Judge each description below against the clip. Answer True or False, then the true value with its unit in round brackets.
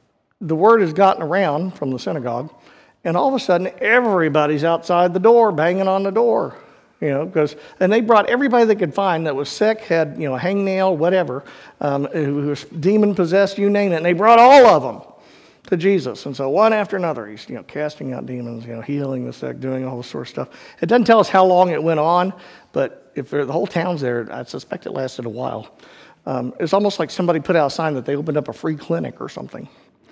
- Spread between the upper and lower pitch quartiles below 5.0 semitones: False (5.3 semitones)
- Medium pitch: True (170 Hz)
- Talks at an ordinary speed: False (230 wpm)